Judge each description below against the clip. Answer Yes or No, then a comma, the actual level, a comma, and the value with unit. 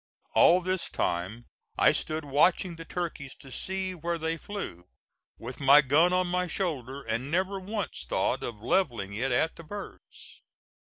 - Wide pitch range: Yes, wide, 5.9 semitones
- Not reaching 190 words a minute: Yes, average, 160 wpm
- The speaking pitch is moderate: Yes, medium, 160 Hz